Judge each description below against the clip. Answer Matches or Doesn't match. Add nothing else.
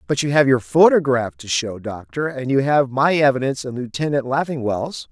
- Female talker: Doesn't match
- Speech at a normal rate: Matches